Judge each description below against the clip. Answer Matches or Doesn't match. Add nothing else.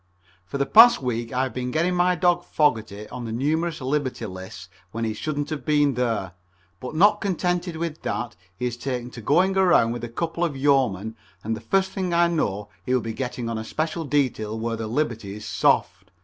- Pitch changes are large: Matches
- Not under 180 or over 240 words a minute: Matches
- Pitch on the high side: Doesn't match